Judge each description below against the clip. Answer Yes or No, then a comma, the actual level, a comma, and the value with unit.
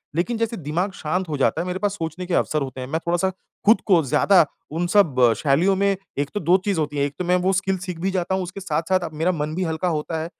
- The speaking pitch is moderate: Yes, medium, 175 Hz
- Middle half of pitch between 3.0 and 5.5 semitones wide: Yes, average, 3.6 semitones